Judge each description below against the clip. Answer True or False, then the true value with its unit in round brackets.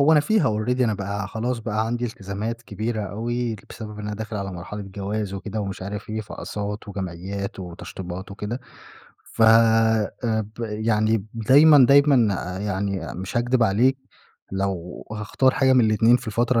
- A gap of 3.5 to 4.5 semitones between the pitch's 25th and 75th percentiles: False (3.1 semitones)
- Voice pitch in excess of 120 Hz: False (110 Hz)